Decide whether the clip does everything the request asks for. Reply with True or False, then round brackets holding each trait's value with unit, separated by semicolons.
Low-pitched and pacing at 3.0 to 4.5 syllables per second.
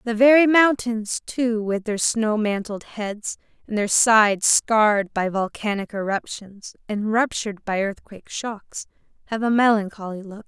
False (215 Hz; 4.3 syllables/s)